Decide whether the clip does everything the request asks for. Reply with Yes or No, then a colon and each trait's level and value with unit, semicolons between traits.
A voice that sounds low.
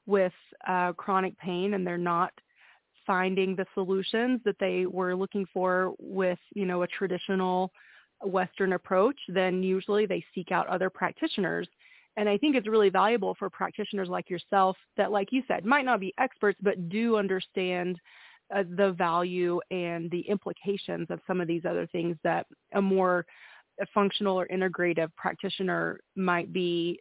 No: high, 190 Hz